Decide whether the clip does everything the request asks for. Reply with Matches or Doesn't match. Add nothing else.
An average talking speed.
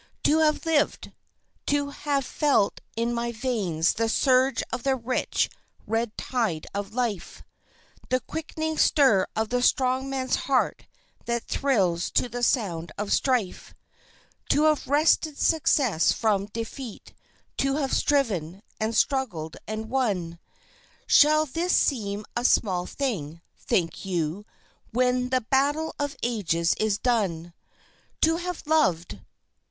Doesn't match